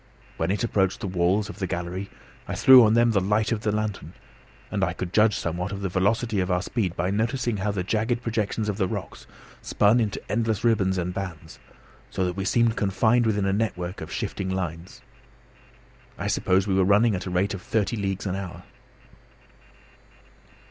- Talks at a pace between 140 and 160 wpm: No, average, 195 wpm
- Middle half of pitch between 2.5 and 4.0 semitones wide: Yes, average, 3.0 semitones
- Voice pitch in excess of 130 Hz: No, low, 100 Hz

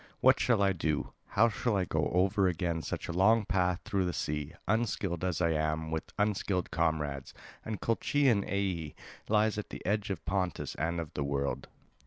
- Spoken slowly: No, average, 185 wpm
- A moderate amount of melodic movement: Yes, average, 4.3 semitones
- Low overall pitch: Yes, very low, 90 Hz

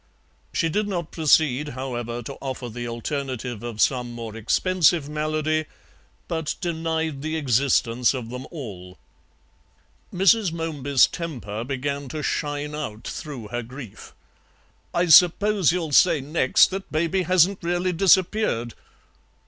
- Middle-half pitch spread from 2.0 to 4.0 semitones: No, average, 5.3 semitones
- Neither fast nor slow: No, slow, 125 wpm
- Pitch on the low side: No, medium, 150 Hz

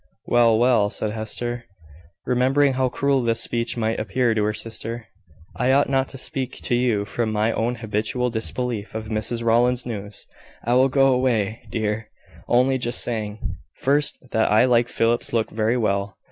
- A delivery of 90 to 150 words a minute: No, average, 170 wpm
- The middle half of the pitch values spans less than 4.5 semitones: Yes, narrow, 2.4 semitones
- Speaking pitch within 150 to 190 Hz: No, low, 120 Hz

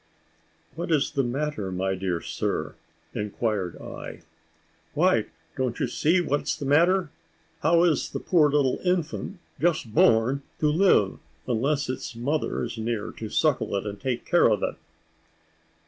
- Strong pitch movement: Yes, wide, 6.0 semitones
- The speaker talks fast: No, average, 150 wpm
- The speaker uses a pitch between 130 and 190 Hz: Yes, low, 135 Hz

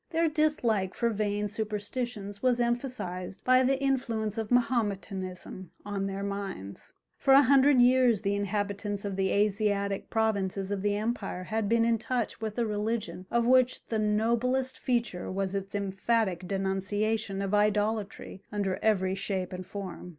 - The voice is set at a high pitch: Yes, high, 210 Hz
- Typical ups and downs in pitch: Yes, average, 3.2 semitones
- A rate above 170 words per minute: No, average, 150 wpm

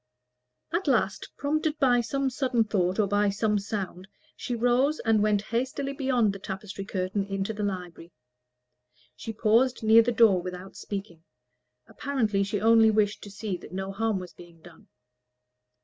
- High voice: Yes, high, 210 Hz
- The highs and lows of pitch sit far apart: No, average, 3.6 semitones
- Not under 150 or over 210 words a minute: Yes, average, 160 wpm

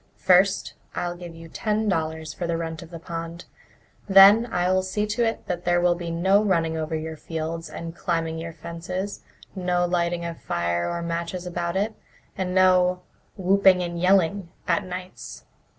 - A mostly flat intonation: Yes, narrow, 2.1 semitones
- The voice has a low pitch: No, medium, 175 Hz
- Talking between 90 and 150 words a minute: No, average, 165 wpm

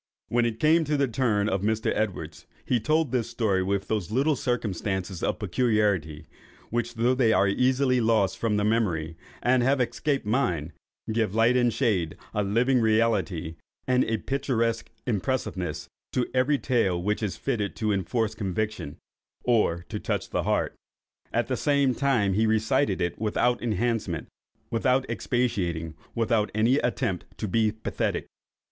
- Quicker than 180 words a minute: No, average, 155 wpm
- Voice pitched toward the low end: Yes, low, 110 Hz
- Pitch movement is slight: No, average, 4.0 semitones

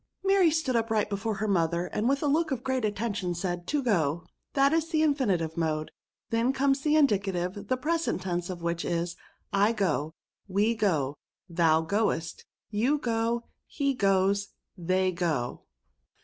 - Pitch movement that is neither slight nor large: No, wide, 7.0 semitones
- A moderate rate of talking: Yes, average, 165 wpm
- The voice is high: Yes, high, 205 Hz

